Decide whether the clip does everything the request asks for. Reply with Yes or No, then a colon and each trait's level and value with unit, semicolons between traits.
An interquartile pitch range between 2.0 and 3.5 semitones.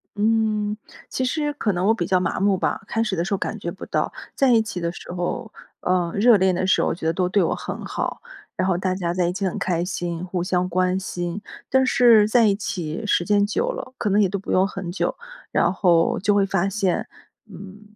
Yes: average, 2.9 semitones